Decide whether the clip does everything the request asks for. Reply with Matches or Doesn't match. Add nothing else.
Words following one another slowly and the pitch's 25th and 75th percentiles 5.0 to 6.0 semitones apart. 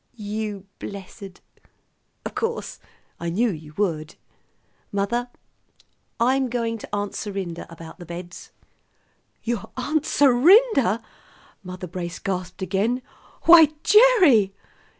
Matches